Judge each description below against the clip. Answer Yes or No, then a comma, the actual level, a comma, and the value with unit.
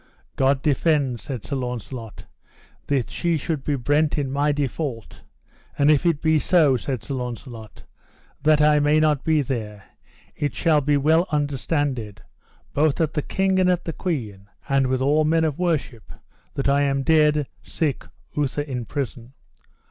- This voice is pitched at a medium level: Yes, medium, 145 Hz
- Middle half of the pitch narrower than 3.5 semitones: Yes, average, 3.0 semitones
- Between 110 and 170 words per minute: Yes, average, 165 wpm